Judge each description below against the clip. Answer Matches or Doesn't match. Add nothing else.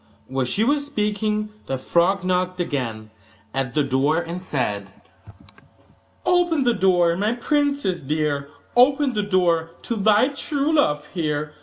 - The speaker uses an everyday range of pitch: Doesn't match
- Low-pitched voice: Doesn't match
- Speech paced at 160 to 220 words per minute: Doesn't match